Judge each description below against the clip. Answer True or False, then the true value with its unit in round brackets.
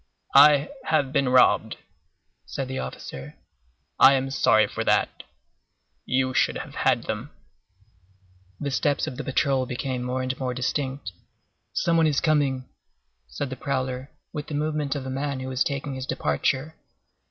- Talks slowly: False (155 wpm)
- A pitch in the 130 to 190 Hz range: True (135 Hz)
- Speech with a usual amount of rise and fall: False (1.8 semitones)